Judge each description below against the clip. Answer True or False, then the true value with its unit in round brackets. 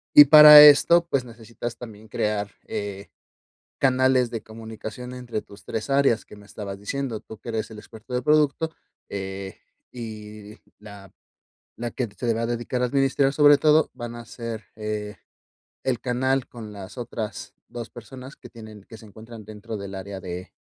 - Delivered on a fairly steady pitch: False (3.4 semitones)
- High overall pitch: False (115 Hz)